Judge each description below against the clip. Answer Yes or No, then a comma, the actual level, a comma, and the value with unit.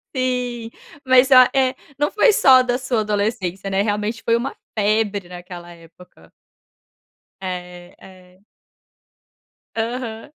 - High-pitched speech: Yes, high, 220 Hz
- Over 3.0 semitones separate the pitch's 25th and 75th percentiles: Yes, average, 5.3 semitones